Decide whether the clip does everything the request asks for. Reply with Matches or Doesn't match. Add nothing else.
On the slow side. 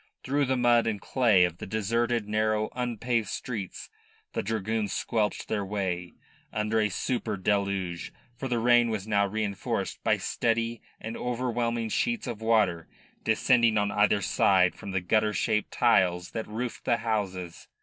Doesn't match